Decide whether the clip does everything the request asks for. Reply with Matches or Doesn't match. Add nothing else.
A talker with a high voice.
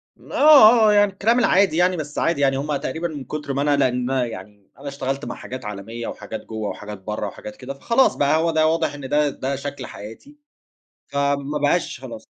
Doesn't match